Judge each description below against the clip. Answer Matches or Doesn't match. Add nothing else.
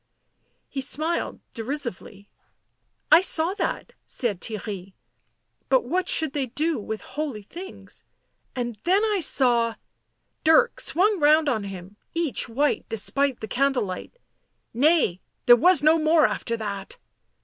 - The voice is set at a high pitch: Matches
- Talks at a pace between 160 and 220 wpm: Doesn't match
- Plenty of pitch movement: Matches